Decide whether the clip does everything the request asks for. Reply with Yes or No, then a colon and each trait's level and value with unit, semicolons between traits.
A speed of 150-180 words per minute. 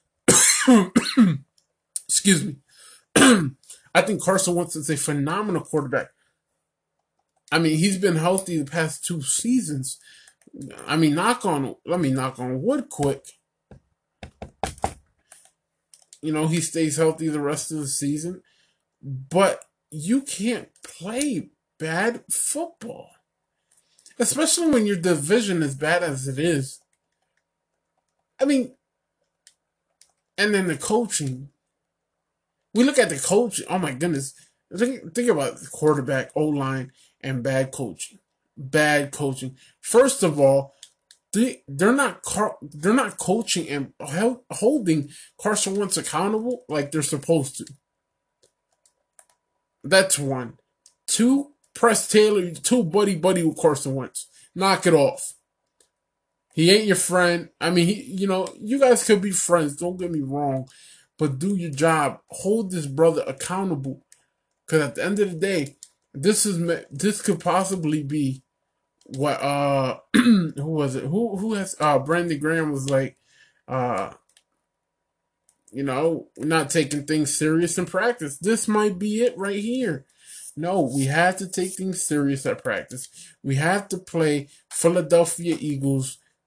No: slow, 135 wpm